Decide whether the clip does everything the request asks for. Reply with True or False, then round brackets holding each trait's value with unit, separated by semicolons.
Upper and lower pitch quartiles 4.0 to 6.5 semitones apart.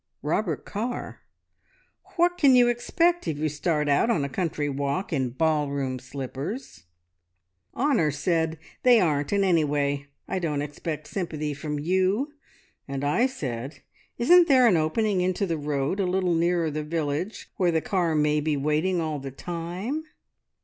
True (5.1 semitones)